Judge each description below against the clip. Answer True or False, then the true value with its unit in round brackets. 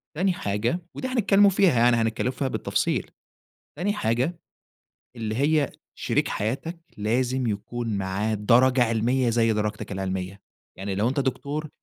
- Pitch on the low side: True (120 Hz)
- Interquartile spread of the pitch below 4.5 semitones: False (5.0 semitones)